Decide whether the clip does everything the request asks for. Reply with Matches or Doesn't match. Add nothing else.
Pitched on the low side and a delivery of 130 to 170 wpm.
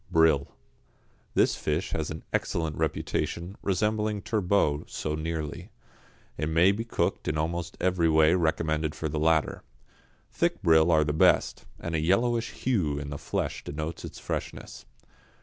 Matches